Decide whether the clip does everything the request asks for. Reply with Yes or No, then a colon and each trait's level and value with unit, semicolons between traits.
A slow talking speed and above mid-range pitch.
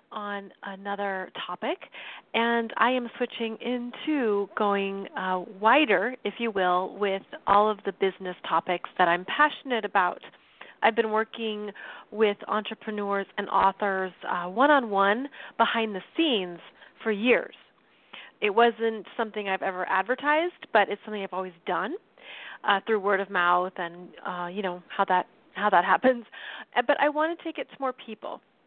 No: average, 155 wpm; high, 210 Hz